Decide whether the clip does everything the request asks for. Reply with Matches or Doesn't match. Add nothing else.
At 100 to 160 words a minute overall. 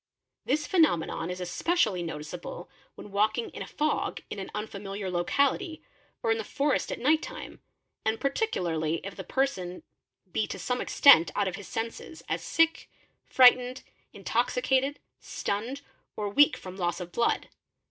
Matches